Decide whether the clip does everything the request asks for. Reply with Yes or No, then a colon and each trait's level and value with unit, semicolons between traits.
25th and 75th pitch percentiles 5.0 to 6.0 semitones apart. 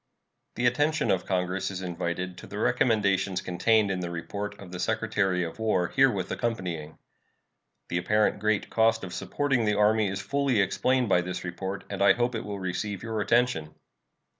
No: average, 3.7 semitones